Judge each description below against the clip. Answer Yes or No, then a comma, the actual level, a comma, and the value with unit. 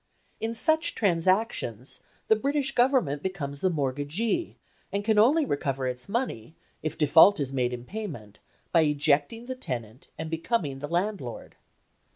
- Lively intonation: Yes, wide, 8.3 semitones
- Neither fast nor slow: Yes, average, 145 wpm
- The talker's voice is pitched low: No, medium, 165 Hz